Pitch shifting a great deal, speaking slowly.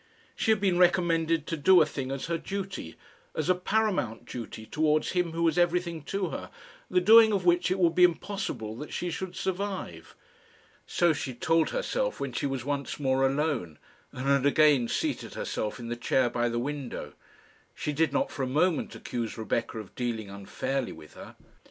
No: wide, 5.9 semitones; average, 190 wpm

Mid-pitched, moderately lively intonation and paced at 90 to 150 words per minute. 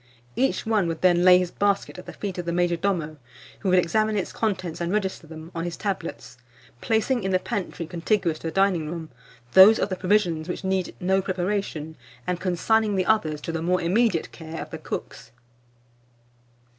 No: medium, 180 Hz; average, 3.1 semitones; average, 195 wpm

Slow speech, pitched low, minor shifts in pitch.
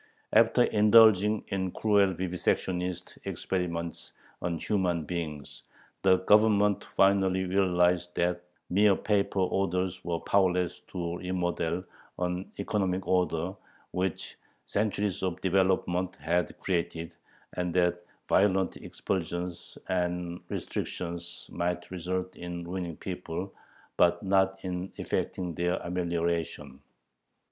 Yes: slow, 100 wpm; very low, 90 Hz; narrow, 1.5 semitones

